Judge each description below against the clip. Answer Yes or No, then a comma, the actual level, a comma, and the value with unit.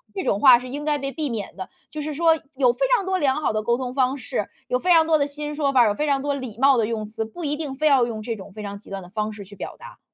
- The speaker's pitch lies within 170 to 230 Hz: No, very high, 265 Hz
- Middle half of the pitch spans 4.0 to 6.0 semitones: Yes, average, 5.3 semitones